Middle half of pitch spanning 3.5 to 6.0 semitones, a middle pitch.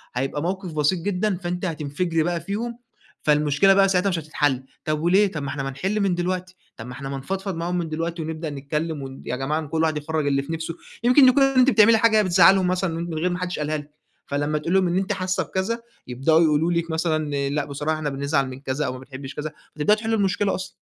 Yes: average, 4.2 semitones; medium, 165 Hz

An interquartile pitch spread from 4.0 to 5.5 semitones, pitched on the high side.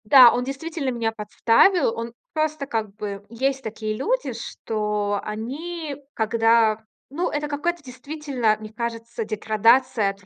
Yes: average, 4.8 semitones; high, 235 Hz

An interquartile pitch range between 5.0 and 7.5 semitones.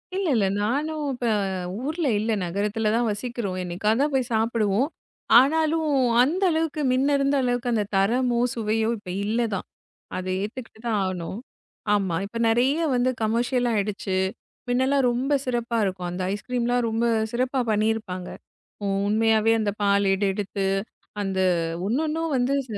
No: average, 4.1 semitones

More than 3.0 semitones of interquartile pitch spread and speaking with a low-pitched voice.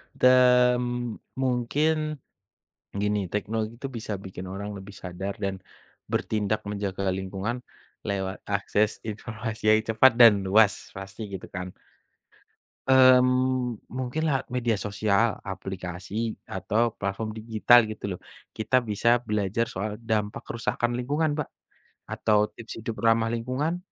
Yes: average, 3.5 semitones; low, 110 Hz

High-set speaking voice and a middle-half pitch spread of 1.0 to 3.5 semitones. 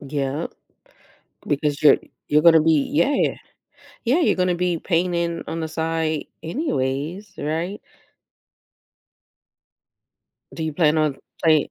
No: medium, 160 Hz; narrow, 2.6 semitones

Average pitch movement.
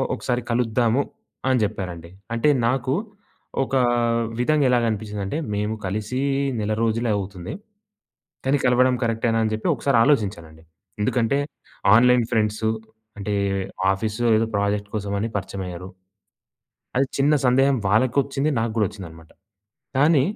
Yes: average, 3.7 semitones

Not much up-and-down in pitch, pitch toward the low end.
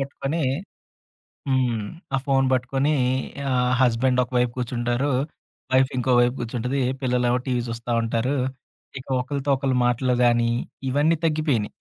Yes: narrow, 2.0 semitones; low, 125 Hz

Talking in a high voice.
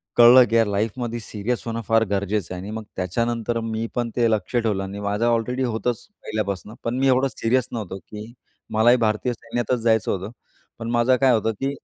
No: low, 115 Hz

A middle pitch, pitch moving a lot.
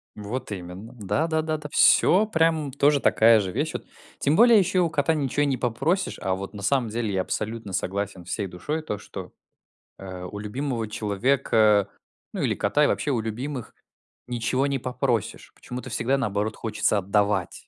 No: low, 115 Hz; wide, 5.9 semitones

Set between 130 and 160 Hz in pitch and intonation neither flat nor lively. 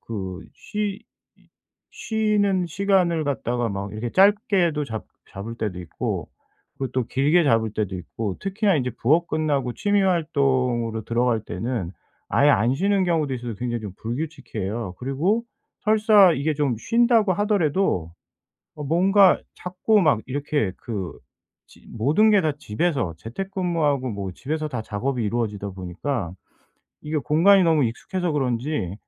No: medium, 140 Hz; wide, 8.1 semitones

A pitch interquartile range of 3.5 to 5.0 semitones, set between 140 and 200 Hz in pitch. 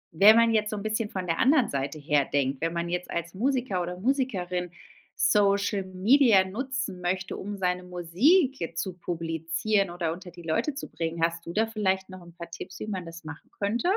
Yes: average, 4.1 semitones; medium, 185 Hz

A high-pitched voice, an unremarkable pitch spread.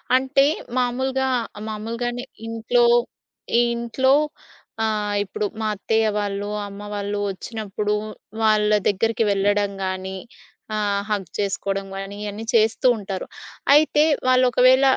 Yes: high, 215 Hz; average, 3.1 semitones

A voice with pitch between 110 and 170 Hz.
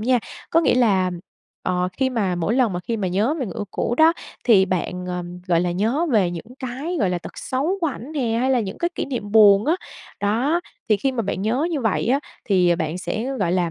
No: high, 220 Hz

